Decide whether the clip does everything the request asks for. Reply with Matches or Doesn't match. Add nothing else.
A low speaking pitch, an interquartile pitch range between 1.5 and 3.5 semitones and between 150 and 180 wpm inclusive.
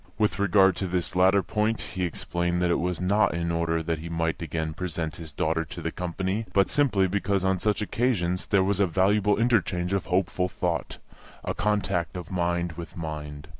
Doesn't match